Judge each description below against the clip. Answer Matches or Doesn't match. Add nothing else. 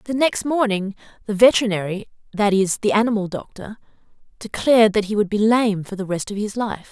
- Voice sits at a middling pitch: Doesn't match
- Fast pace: Doesn't match